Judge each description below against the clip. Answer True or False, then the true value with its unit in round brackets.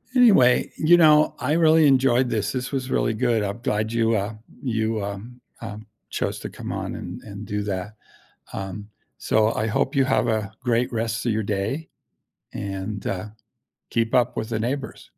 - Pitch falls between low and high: False (115 Hz)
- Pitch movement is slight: False (3.4 semitones)